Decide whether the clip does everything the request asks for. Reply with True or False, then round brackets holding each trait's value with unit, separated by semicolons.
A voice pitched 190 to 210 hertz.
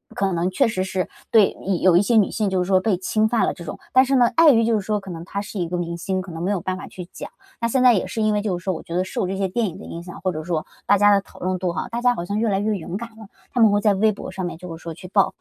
True (195 Hz)